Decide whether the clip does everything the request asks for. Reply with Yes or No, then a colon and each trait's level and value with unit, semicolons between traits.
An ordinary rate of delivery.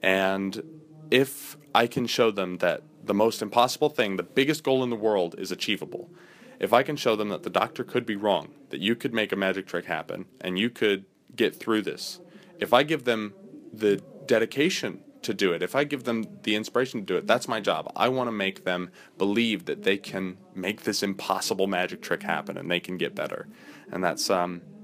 No: fast, 215 wpm